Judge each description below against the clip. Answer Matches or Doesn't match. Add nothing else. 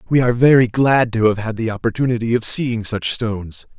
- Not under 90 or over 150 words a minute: Doesn't match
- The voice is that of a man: Matches